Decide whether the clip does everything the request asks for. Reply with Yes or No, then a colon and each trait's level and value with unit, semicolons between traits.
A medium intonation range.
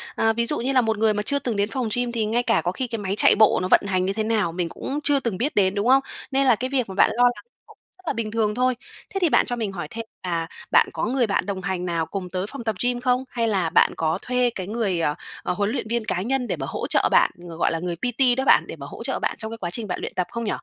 Yes: average, 4.6 semitones